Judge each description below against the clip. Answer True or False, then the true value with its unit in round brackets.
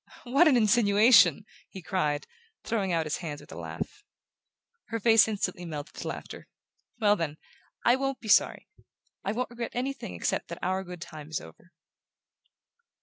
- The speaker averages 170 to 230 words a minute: False (160 wpm)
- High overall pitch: True (200 Hz)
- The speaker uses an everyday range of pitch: False (6.1 semitones)